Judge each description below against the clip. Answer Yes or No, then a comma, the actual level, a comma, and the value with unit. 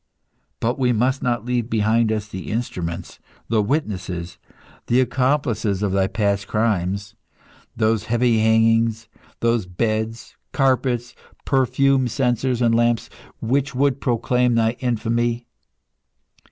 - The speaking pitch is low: Yes, low, 115 Hz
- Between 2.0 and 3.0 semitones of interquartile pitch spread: Yes, narrow, 2.6 semitones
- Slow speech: Yes, slow, 115 wpm